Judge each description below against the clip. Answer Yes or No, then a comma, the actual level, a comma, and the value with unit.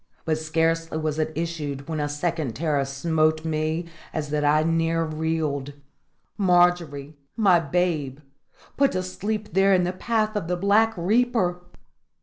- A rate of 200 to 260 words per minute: No, average, 145 wpm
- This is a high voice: No, medium, 165 Hz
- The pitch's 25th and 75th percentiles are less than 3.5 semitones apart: Yes, average, 2.7 semitones